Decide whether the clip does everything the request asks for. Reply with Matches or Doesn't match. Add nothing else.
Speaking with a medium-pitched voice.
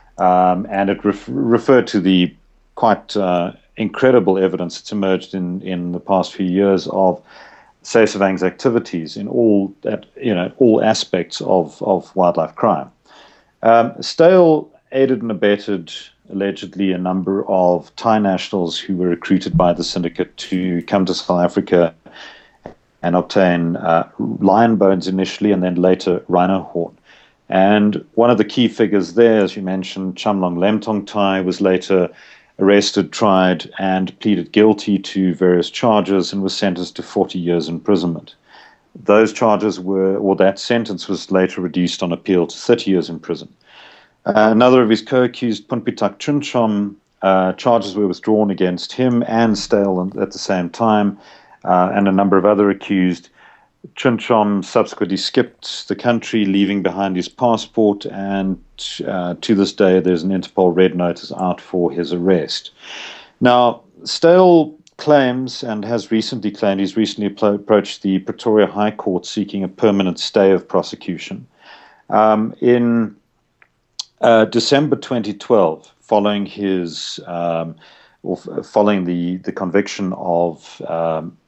Doesn't match